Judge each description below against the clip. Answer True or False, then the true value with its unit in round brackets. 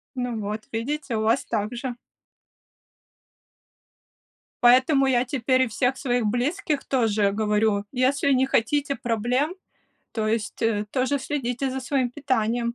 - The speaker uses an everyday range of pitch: True (3.2 semitones)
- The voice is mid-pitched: False (245 Hz)